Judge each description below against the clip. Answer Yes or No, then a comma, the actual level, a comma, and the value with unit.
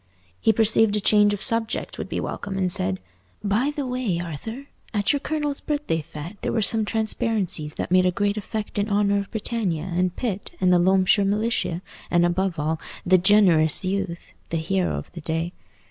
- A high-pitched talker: Yes, high, 195 Hz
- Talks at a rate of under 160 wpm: No, average, 190 wpm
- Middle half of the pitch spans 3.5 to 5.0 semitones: Yes, average, 3.9 semitones